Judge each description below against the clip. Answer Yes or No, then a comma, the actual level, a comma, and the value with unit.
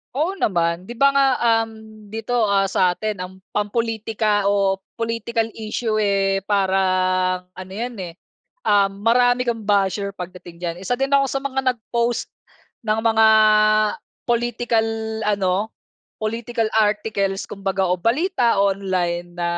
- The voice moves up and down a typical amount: Yes, average, 3.3 semitones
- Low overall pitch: No, high, 210 Hz